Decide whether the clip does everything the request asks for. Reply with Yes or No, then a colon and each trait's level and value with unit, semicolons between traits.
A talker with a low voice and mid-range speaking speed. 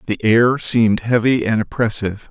Yes: low, 115 Hz; average, 155 wpm